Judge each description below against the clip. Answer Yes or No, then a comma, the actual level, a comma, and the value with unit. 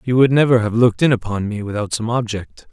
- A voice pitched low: Yes, low, 115 Hz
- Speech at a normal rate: No, fast, 245 wpm